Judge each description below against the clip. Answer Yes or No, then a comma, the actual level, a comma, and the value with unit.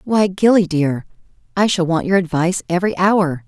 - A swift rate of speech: No, average, 175 wpm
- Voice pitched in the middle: Yes, medium, 180 Hz